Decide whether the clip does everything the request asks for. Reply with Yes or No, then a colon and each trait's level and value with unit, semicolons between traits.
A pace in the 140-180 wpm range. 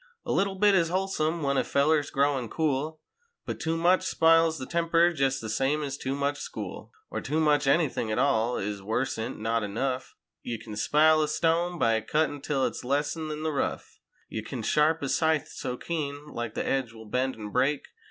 No: average, 200 wpm